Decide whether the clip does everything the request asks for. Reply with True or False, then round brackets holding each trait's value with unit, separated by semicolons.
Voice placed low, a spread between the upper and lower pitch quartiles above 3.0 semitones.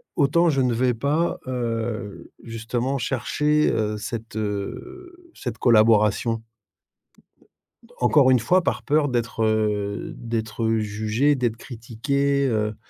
True (120 Hz; 4.1 semitones)